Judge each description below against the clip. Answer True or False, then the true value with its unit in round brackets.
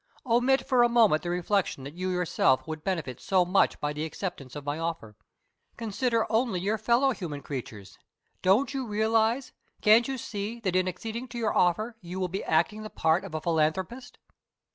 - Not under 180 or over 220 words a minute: True (185 wpm)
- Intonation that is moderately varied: False (5.9 semitones)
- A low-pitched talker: False (190 Hz)